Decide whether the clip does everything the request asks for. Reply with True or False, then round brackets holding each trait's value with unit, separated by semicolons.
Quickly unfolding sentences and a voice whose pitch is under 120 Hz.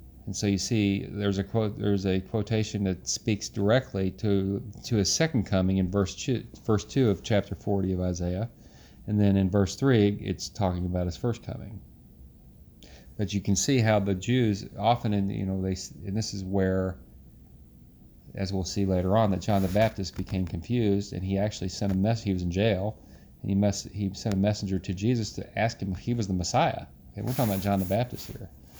True (210 wpm; 100 Hz)